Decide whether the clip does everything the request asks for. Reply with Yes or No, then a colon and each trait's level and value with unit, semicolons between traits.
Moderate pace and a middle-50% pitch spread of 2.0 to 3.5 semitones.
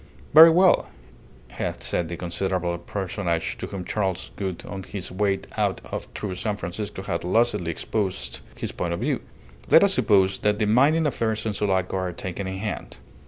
Yes: average, 170 wpm; average, 2.8 semitones